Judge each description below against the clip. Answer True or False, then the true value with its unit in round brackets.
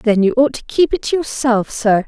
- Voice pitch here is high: True (240 Hz)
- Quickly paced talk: True (260 wpm)